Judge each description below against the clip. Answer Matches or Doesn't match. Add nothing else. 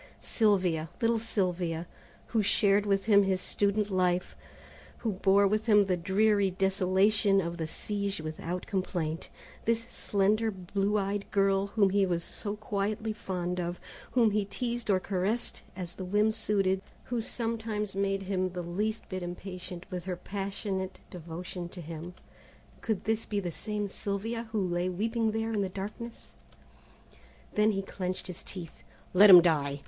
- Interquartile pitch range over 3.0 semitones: Doesn't match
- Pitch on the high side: Matches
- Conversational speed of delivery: Matches